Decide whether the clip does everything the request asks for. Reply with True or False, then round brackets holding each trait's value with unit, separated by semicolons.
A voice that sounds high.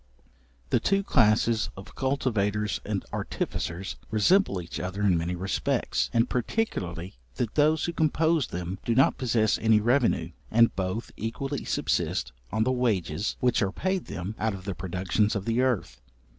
False (110 Hz)